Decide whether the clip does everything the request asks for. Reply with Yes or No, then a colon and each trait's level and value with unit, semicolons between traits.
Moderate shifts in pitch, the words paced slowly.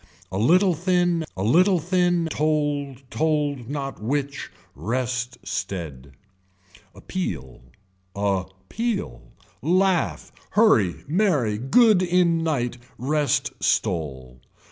No: wide, 8.5 semitones; slow, 95 wpm